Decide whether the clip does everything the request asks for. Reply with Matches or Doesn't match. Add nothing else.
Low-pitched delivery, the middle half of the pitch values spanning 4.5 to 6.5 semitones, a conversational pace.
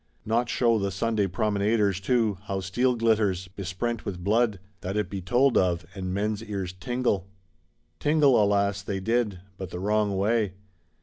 Doesn't match